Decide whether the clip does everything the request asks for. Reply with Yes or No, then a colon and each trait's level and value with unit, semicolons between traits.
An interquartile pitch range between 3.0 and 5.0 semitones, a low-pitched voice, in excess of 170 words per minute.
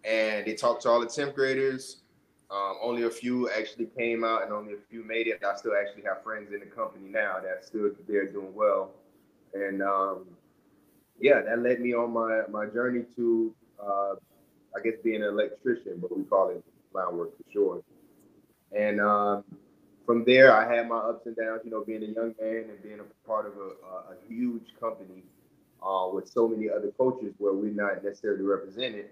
No: narrow, 2.5 semitones; low, 110 Hz; average, 200 wpm